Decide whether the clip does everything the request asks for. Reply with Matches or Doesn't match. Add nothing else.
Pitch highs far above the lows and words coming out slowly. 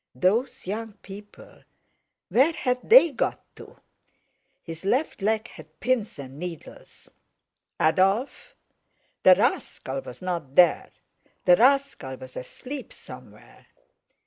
Matches